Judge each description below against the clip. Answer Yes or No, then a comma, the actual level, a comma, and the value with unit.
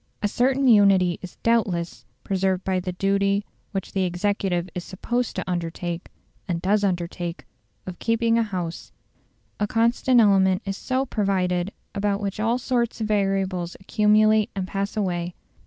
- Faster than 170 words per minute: No, average, 150 wpm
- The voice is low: No, high, 195 Hz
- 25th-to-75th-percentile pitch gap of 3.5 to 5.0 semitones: No, average, 2.8 semitones